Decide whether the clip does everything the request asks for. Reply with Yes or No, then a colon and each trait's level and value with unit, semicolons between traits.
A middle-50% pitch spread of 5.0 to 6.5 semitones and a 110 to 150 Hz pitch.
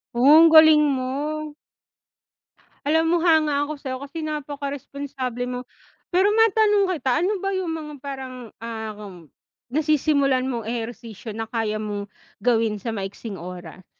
No: wide, 5.5 semitones; very high, 265 Hz